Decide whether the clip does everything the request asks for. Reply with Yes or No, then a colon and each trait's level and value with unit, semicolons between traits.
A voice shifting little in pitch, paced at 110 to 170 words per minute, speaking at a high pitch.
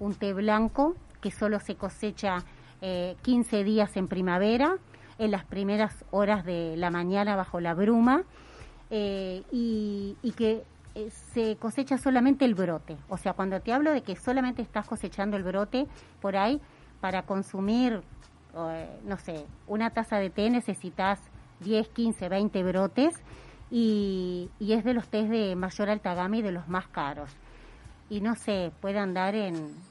No: average, 3.2 semitones; average, 165 wpm; high, 205 Hz